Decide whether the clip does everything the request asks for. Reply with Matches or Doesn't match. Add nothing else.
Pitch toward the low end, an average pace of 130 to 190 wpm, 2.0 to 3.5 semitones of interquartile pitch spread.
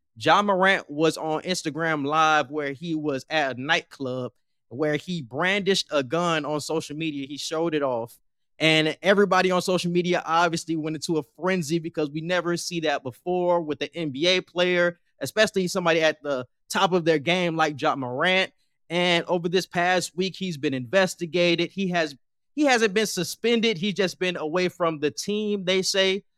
Doesn't match